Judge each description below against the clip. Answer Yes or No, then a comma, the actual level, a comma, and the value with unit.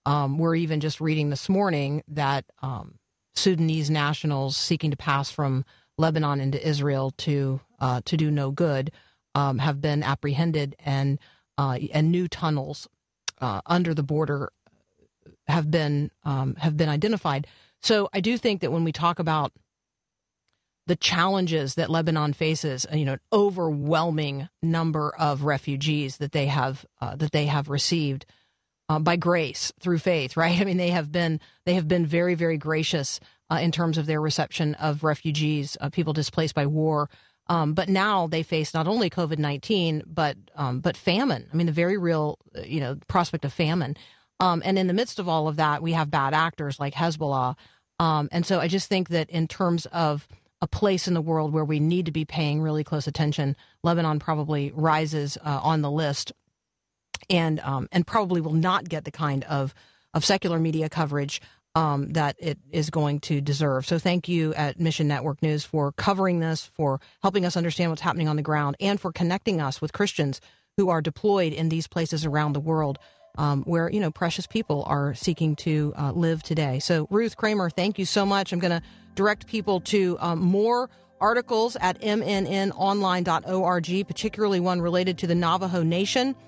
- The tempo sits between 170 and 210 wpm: Yes, average, 180 wpm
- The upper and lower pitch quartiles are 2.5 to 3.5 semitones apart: Yes, average, 3.0 semitones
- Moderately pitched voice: Yes, medium, 160 Hz